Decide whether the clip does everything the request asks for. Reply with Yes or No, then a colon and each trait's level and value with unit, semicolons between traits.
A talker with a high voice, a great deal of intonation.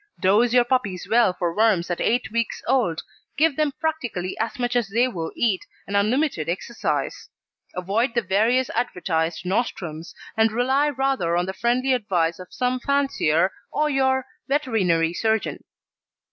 Yes: high, 225 Hz; wide, 5.9 semitones